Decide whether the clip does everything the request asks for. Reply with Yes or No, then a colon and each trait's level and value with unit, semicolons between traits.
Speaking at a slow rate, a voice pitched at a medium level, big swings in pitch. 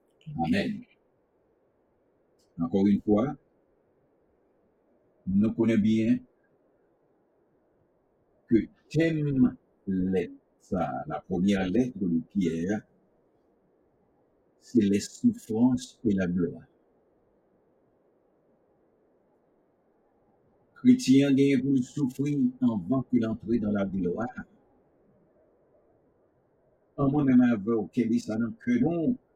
No: slow, 80 wpm; low, 120 Hz; wide, 5.7 semitones